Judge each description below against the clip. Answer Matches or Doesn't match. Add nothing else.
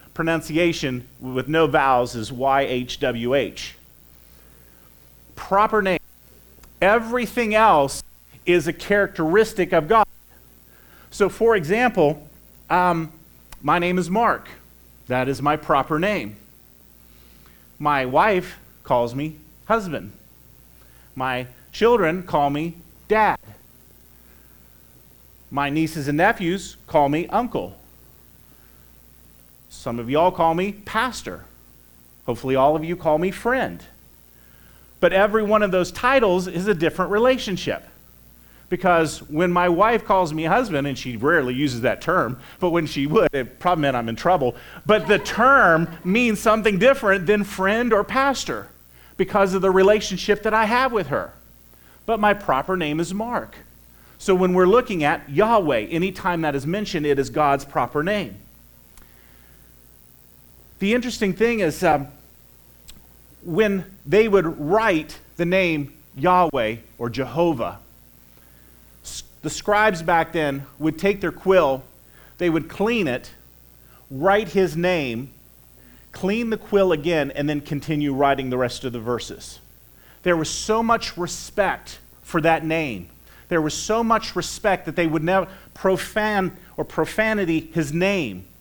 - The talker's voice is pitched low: Doesn't match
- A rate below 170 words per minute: Matches